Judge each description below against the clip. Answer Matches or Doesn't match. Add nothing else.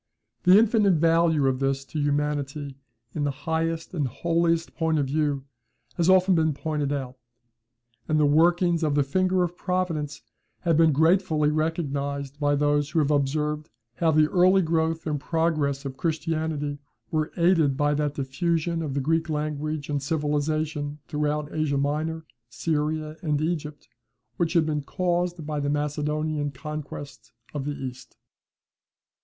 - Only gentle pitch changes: Matches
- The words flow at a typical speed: Matches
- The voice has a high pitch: Doesn't match